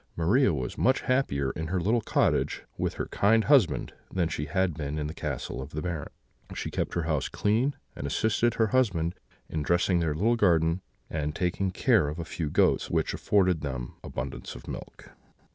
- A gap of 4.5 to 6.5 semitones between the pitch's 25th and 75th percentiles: Yes, wide, 5.6 semitones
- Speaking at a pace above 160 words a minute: Yes, average, 190 wpm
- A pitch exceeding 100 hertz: No, very low, 85 Hz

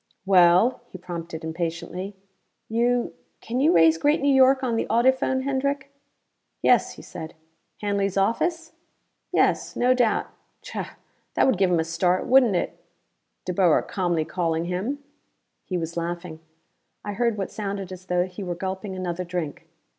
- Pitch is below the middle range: No, high, 190 Hz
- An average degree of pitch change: No, wide, 5.7 semitones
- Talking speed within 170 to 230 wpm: No, average, 155 wpm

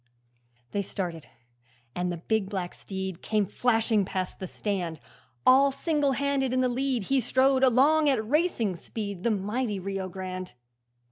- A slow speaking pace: No, average, 150 wpm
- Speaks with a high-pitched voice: Yes, high, 215 Hz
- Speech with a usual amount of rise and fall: No, wide, 5.7 semitones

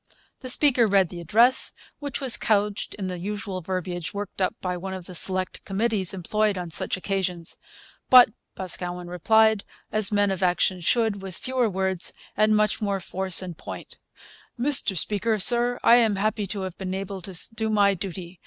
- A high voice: Yes, high, 195 Hz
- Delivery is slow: No, average, 180 wpm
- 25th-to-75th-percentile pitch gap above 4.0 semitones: No, average, 2.8 semitones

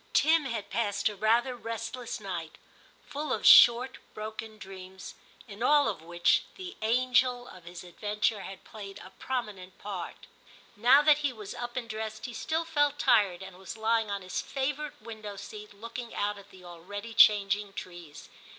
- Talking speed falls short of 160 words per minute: No, average, 170 wpm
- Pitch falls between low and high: No, high, 215 Hz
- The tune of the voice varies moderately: Yes, average, 3.9 semitones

